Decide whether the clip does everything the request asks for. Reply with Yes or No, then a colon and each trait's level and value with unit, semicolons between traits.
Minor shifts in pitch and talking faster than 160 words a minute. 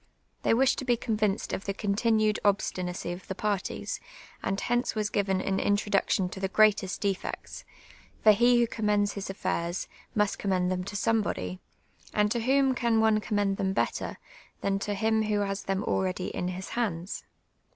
Yes: narrow, 2.3 semitones; average, 170 wpm